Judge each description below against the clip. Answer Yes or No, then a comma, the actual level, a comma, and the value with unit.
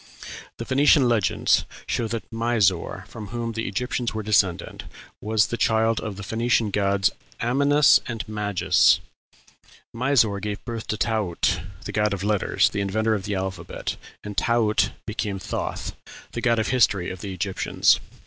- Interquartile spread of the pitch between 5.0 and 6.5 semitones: No, average, 2.7 semitones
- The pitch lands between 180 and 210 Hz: No, low, 110 Hz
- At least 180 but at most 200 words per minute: No, average, 155 wpm